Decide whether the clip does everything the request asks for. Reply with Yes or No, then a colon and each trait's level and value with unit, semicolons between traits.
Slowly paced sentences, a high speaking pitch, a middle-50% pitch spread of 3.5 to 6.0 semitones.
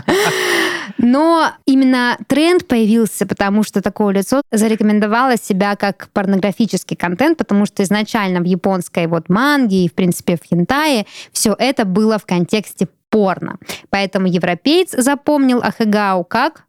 No: average, 130 wpm; high, 210 Hz; average, 4.2 semitones